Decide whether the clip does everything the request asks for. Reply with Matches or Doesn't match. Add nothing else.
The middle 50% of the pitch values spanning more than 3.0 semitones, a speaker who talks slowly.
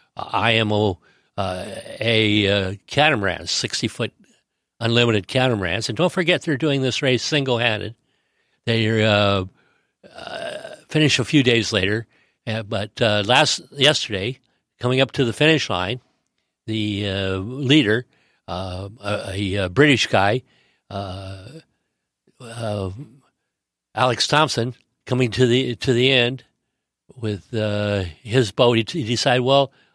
Matches